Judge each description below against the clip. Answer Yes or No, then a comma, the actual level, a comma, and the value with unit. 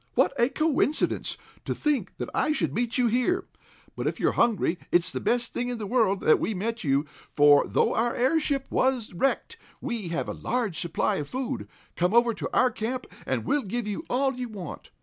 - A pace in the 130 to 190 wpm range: No, fast, 205 wpm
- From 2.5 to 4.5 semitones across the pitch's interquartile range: No, average, 4.9 semitones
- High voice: Yes, high, 235 Hz